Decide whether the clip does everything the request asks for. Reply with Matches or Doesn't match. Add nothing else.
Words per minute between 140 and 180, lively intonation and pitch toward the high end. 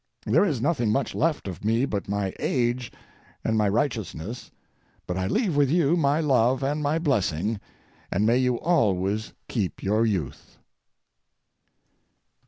Doesn't match